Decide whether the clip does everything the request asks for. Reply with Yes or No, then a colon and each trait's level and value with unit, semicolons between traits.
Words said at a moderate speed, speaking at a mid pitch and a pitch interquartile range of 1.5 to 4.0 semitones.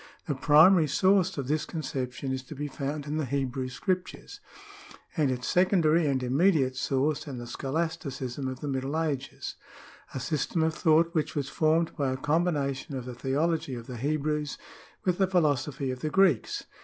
Yes: average, 180 wpm; medium, 145 Hz; average, 3.5 semitones